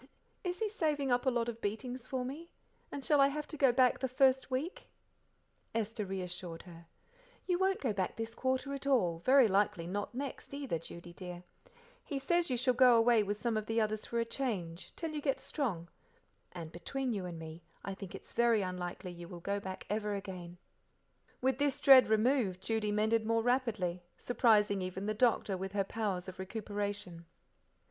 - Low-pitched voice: No, high, 220 Hz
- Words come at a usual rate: Yes, average, 190 wpm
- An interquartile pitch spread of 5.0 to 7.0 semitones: Yes, wide, 5.6 semitones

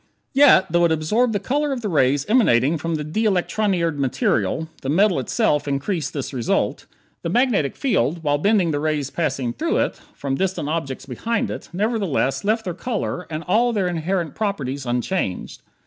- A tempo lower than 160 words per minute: No, average, 175 wpm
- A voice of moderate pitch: Yes, medium, 165 Hz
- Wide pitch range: Yes, wide, 6.6 semitones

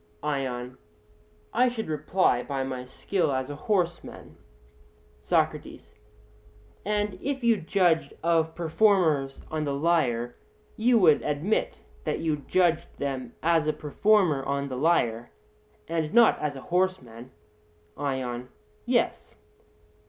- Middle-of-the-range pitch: Yes, medium, 155 Hz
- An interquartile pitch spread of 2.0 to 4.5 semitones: No, average, 5.3 semitones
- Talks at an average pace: No, slow, 125 wpm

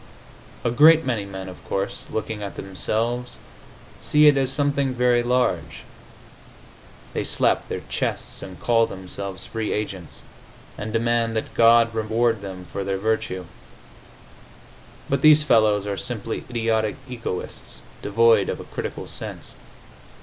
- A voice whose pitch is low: Yes, low, 115 Hz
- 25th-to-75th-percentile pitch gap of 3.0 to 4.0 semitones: Yes, average, 3.5 semitones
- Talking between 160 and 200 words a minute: No, slow, 135 wpm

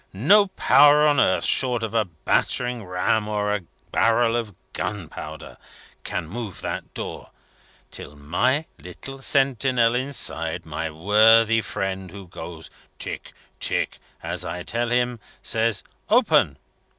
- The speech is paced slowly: Yes, slow, 125 wpm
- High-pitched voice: No, low, 110 Hz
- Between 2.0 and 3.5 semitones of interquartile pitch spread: No, average, 5.3 semitones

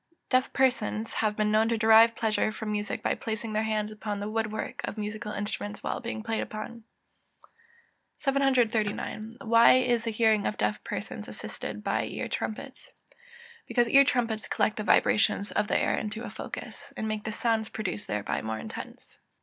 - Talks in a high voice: Yes, high, 220 Hz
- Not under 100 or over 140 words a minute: No, average, 180 wpm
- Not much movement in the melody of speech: Yes, narrow, 1.6 semitones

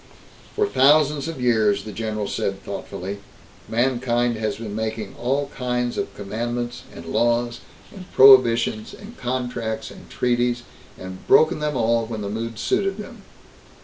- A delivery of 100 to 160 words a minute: Yes, average, 145 wpm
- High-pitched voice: No, low, 120 Hz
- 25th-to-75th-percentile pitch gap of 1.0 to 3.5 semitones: Yes, average, 3.0 semitones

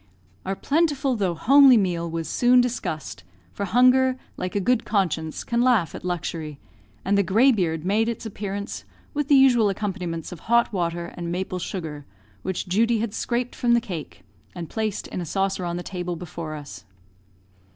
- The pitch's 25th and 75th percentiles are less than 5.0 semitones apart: No, wide, 5.6 semitones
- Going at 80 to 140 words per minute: No, average, 170 wpm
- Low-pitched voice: No, high, 195 Hz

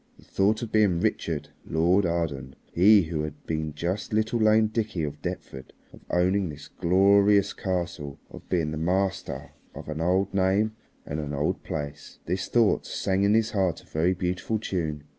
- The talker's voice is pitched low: Yes, very low, 90 Hz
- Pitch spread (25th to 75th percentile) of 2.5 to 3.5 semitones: No, average, 4.4 semitones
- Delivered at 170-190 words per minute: Yes, average, 175 wpm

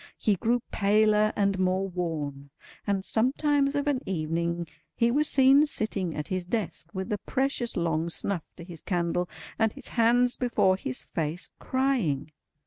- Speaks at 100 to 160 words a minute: Yes, average, 155 wpm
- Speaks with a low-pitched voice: No, high, 195 Hz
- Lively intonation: Yes, wide, 6.0 semitones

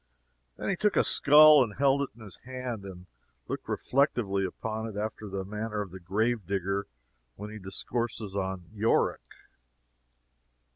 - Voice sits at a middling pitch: No, low, 105 Hz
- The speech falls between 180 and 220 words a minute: No, average, 155 wpm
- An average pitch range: Yes, average, 3.8 semitones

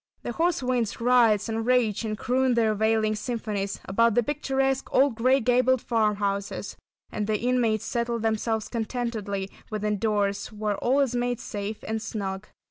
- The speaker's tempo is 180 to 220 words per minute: No, average, 155 wpm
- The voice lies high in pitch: Yes, high, 225 Hz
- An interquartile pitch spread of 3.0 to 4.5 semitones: No, narrow, 2.6 semitones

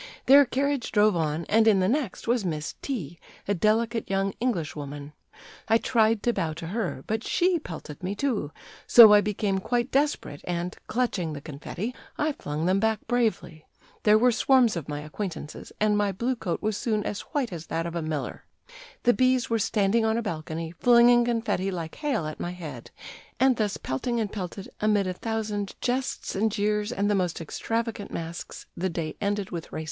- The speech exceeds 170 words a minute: Yes, average, 195 wpm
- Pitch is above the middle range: Yes, high, 205 Hz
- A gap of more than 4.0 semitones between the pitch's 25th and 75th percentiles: Yes, wide, 5.4 semitones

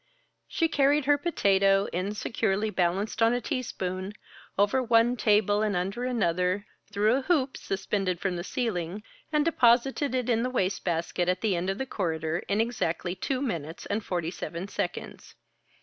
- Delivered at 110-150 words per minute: No, average, 160 wpm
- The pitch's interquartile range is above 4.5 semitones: Yes, average, 5.1 semitones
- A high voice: Yes, high, 205 Hz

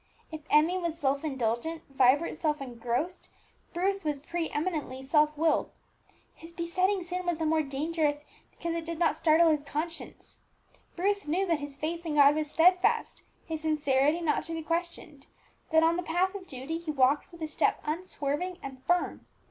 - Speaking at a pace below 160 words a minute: No, average, 175 wpm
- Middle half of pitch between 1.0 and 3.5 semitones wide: Yes, average, 2.7 semitones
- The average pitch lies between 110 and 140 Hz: No, very high, 320 Hz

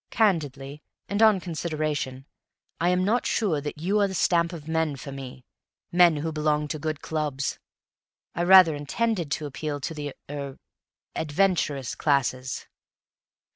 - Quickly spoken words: No, average, 145 wpm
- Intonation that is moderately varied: Yes, average, 3.6 semitones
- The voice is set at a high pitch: No, medium, 155 Hz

